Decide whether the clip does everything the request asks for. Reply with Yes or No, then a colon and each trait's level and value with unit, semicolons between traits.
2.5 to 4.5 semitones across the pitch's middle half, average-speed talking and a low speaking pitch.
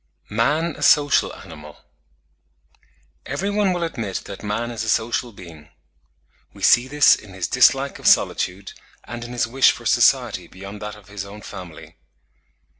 No: average, 5.3 semitones; average, 160 wpm; low, 110 Hz